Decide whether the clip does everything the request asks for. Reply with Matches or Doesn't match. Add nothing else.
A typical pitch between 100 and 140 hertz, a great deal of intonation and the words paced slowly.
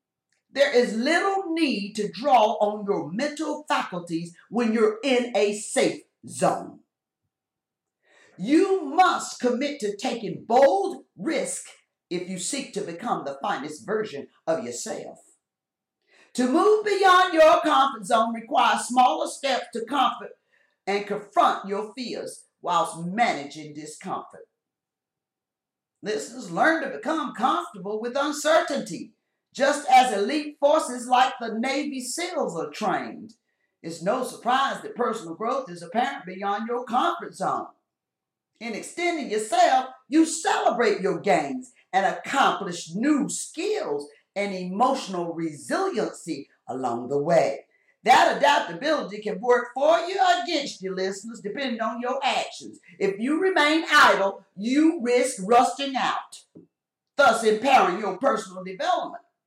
Doesn't match